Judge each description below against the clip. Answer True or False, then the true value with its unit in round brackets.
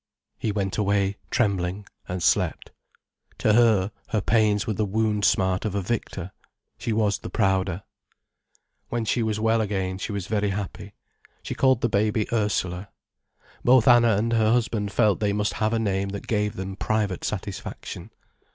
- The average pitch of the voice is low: True (105 Hz)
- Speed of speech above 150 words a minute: True (165 wpm)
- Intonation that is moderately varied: False (2.1 semitones)